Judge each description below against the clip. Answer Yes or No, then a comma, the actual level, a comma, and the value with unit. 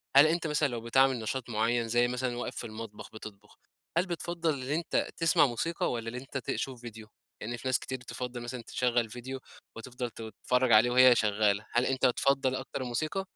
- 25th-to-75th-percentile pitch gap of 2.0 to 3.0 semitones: Yes, narrow, 2.4 semitones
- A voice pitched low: Yes, low, 125 Hz